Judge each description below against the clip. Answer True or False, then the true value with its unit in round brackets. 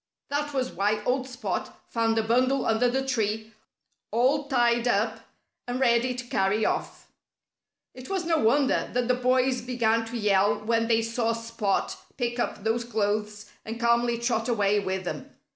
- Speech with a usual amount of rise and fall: False (2.3 semitones)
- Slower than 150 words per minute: False (165 wpm)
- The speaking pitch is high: True (235 Hz)